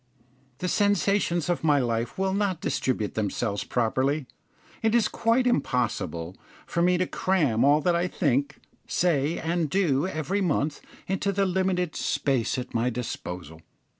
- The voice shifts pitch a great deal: Yes, wide, 7.0 semitones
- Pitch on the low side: No, medium, 155 Hz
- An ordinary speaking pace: Yes, average, 145 wpm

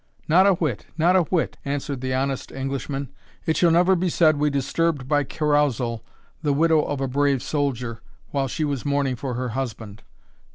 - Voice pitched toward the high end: No, medium, 140 Hz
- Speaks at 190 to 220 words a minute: No, average, 180 wpm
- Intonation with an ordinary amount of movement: Yes, average, 3.1 semitones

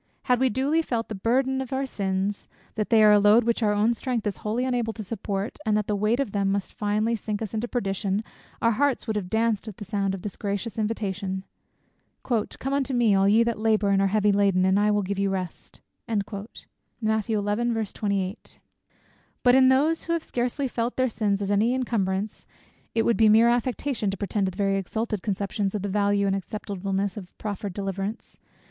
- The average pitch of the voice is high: Yes, high, 210 Hz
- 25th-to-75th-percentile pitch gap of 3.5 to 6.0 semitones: No, average, 2.9 semitones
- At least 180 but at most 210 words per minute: Yes, average, 200 wpm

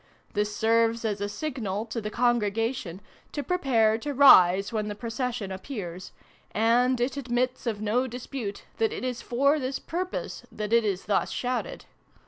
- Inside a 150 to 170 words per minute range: Yes, average, 160 wpm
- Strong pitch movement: No, average, 3.4 semitones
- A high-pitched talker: Yes, high, 230 Hz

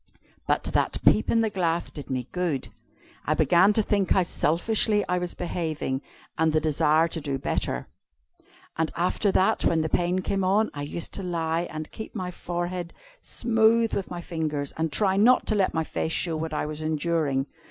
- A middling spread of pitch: Yes, average, 3.3 semitones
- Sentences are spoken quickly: No, average, 190 wpm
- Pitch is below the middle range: No, medium, 170 Hz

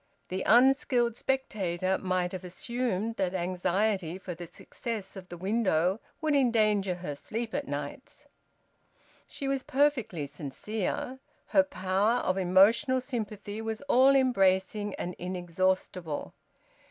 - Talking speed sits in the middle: No, slow, 120 wpm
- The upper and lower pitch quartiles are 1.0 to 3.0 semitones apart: No, average, 4.7 semitones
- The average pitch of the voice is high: Yes, high, 200 Hz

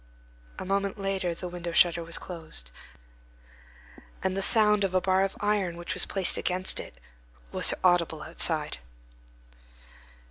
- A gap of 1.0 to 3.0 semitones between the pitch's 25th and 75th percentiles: Yes, narrow, 2.4 semitones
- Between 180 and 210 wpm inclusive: No, average, 140 wpm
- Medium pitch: Yes, medium, 180 Hz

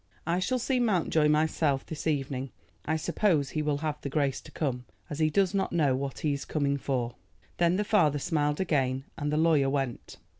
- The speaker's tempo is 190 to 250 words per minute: Yes, average, 200 wpm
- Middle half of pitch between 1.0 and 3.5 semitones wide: Yes, average, 3.1 semitones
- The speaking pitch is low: No, medium, 150 Hz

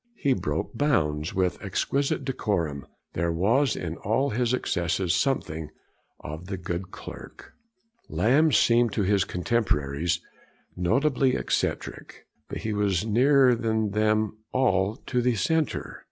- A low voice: Yes, low, 105 Hz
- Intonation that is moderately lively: No, wide, 6.5 semitones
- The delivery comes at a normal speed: No, slow, 125 wpm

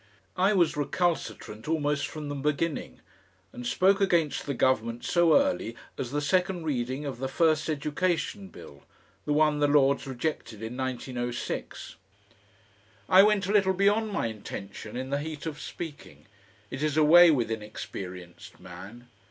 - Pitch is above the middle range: No, medium, 145 Hz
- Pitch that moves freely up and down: Yes, wide, 6.0 semitones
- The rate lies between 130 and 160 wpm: Yes, average, 150 wpm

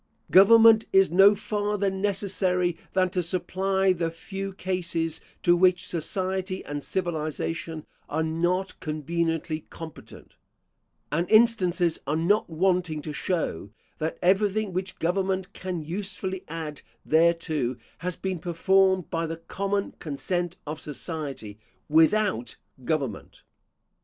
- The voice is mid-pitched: Yes, medium, 180 Hz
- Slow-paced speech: Yes, slow, 115 wpm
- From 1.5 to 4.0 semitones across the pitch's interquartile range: Yes, average, 3.0 semitones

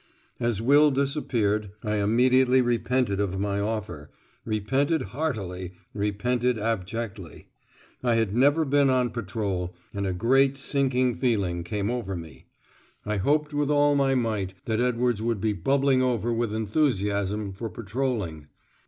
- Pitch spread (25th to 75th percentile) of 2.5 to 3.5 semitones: No, average, 4.4 semitones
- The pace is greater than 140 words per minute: No, slow, 135 wpm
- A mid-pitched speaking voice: No, low, 115 Hz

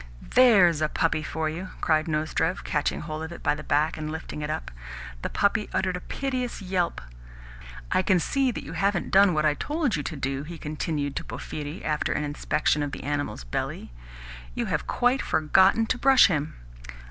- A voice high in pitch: No, medium, 160 Hz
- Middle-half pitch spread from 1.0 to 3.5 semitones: No, average, 4.6 semitones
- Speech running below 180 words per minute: No, average, 195 wpm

